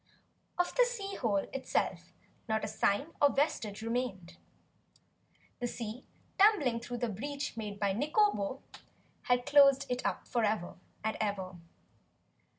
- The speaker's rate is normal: No, slow, 130 wpm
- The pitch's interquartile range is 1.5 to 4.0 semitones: No, average, 5.2 semitones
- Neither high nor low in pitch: No, high, 245 Hz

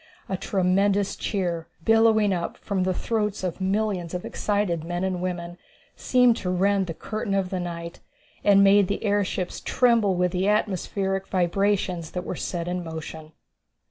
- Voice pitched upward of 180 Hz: Yes, high, 190 Hz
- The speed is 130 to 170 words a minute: Yes, average, 160 wpm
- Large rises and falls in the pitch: No, narrow, 2.4 semitones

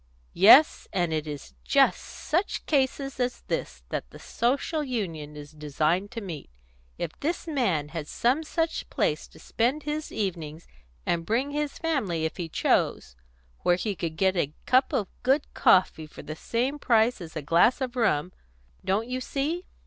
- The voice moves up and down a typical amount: No, wide, 8.9 semitones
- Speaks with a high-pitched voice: Yes, high, 210 Hz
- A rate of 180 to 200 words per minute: No, average, 170 wpm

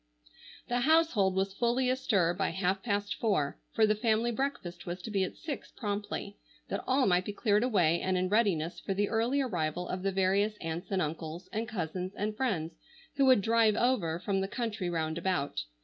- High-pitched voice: Yes, high, 200 Hz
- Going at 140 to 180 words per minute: No, average, 195 wpm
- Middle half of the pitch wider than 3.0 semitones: Yes, average, 4.2 semitones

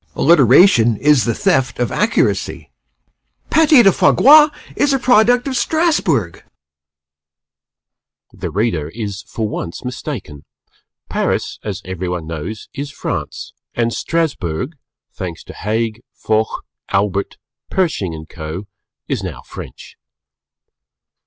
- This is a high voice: No, low, 115 Hz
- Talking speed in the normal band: No, slow, 120 wpm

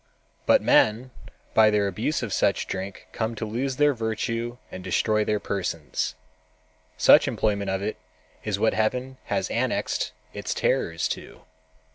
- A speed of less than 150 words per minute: Yes, average, 140 wpm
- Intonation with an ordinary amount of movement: Yes, average, 3.5 semitones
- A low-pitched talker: Yes, low, 105 Hz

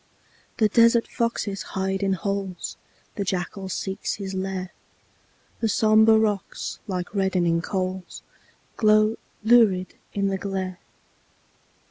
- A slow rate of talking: Yes, slow, 110 wpm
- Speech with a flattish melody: Yes, narrow, 2.3 semitones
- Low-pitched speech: No, high, 195 Hz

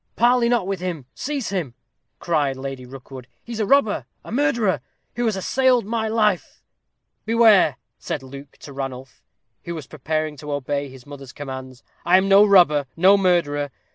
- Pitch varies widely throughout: Yes, wide, 7.7 semitones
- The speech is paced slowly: No, average, 170 wpm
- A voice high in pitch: No, medium, 170 Hz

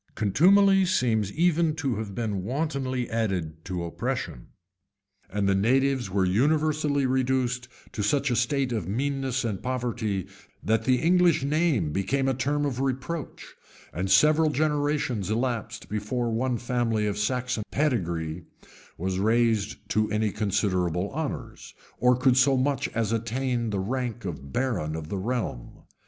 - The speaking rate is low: No, average, 145 wpm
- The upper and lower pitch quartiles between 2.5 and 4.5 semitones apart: No, average, 5.0 semitones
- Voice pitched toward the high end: No, low, 120 Hz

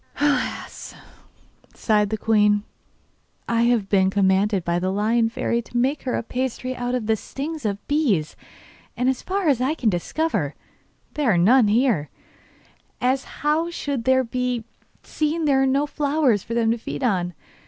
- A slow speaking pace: No, average, 165 wpm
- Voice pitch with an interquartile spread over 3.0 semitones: Yes, average, 4.7 semitones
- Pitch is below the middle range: No, high, 240 Hz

